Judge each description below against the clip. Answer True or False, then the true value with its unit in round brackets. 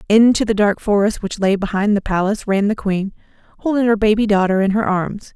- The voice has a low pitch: False (205 Hz)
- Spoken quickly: True (215 wpm)